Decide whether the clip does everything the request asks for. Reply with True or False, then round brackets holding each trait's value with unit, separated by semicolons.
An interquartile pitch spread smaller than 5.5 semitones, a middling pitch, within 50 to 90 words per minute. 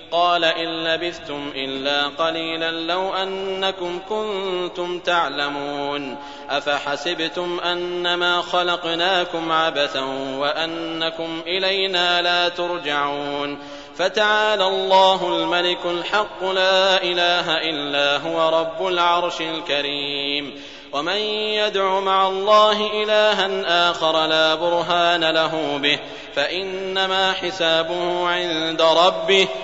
True (2.9 semitones; 175 Hz; 85 wpm)